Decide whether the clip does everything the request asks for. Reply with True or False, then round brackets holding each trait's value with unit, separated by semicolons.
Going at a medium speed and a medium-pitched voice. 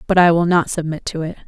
False (285 wpm; 170 Hz)